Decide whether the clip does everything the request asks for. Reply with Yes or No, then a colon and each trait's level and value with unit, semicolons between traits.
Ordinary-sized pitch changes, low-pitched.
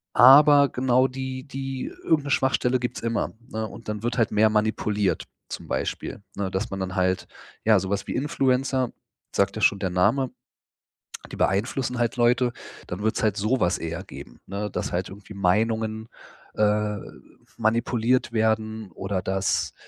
Yes: average, 3.9 semitones; low, 110 Hz